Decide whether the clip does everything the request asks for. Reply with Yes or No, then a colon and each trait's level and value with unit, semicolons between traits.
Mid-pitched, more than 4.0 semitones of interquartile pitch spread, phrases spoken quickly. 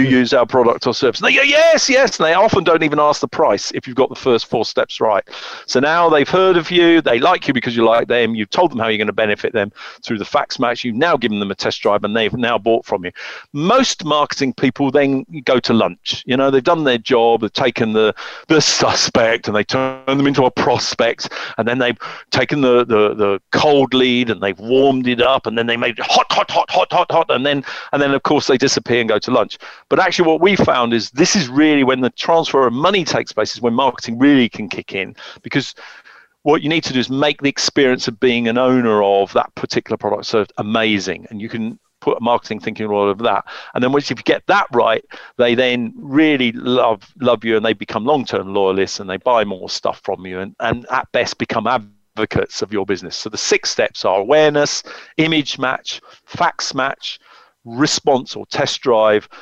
No: low, 130 Hz; average, 4.6 semitones; fast, 230 wpm